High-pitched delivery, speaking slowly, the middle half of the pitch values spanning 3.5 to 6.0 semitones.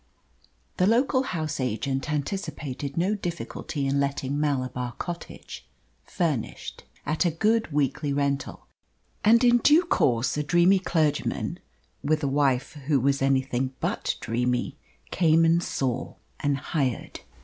No: medium, 145 Hz; slow, 125 wpm; average, 4.2 semitones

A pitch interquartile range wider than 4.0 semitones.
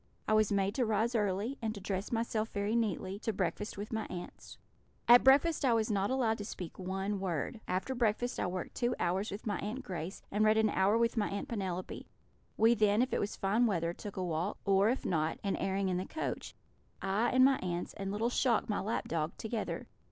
No: average, 3.1 semitones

